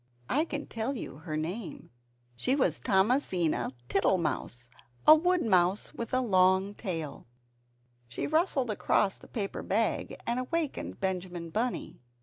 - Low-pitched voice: No, high, 200 Hz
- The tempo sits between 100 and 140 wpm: Yes, slow, 135 wpm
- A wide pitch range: Yes, wide, 6.3 semitones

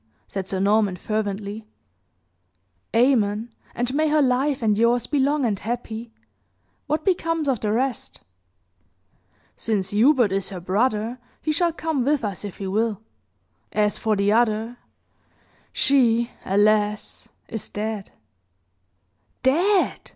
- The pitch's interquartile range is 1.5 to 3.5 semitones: No, average, 4.2 semitones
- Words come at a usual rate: No, slow, 125 wpm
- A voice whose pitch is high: Yes, high, 225 Hz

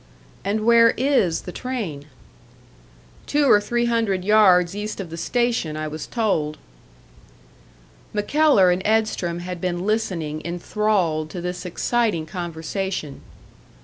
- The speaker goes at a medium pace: No, slow, 120 wpm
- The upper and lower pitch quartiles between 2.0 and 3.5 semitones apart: No, average, 4.5 semitones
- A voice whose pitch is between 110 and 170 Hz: No, high, 190 Hz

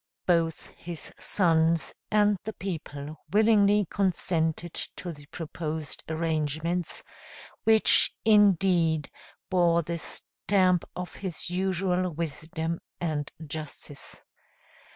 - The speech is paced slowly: Yes, slow, 90 wpm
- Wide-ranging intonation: No, average, 2.9 semitones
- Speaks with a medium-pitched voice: Yes, medium, 170 Hz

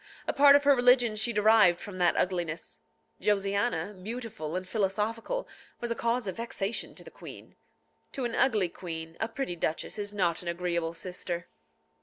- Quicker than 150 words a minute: Yes, average, 170 wpm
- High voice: Yes, high, 205 Hz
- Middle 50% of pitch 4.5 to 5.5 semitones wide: Yes, average, 4.9 semitones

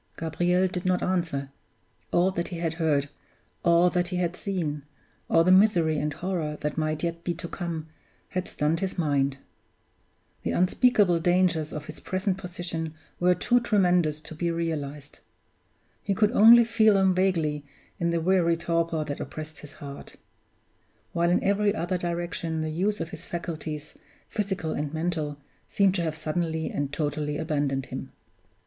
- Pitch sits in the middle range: Yes, medium, 170 Hz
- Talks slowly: No, average, 160 wpm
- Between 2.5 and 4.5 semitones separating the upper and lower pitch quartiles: Yes, average, 2.9 semitones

